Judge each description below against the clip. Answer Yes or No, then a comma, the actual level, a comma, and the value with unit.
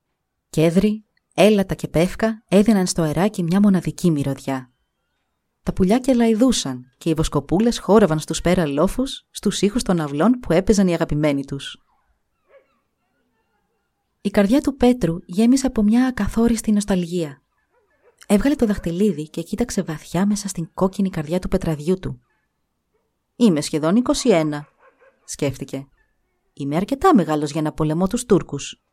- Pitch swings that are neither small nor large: No, wide, 6.0 semitones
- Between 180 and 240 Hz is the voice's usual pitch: Yes, medium, 185 Hz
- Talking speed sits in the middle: Yes, average, 135 wpm